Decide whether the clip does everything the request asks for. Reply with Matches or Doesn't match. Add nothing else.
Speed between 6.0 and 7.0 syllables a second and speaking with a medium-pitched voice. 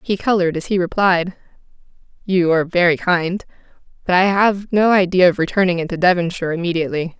Matches